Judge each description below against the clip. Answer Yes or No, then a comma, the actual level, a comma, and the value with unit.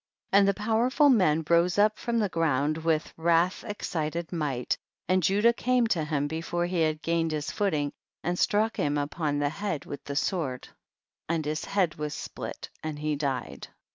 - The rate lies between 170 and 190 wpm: Yes, average, 185 wpm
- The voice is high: No, medium, 165 Hz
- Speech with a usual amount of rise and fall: Yes, average, 4.7 semitones